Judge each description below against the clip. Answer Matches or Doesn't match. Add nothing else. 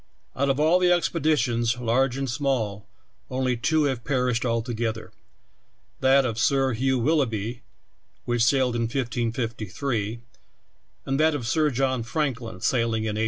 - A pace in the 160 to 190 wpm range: Doesn't match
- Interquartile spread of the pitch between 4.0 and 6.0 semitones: Doesn't match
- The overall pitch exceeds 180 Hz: Doesn't match